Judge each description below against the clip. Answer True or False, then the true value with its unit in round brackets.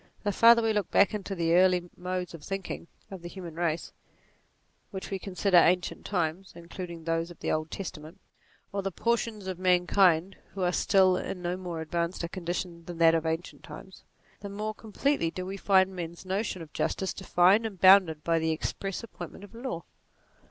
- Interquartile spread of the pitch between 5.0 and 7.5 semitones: False (2.6 semitones)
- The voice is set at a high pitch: False (180 Hz)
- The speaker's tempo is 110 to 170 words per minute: False (190 wpm)